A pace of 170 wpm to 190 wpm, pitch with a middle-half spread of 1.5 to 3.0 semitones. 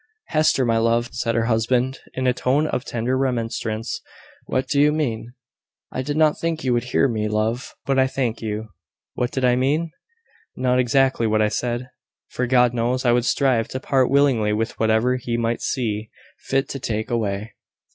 Yes: average, 185 wpm; narrow, 2.5 semitones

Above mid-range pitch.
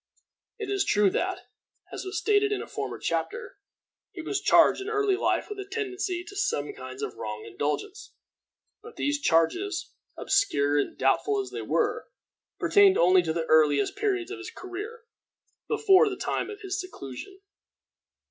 Yes: very high, 390 Hz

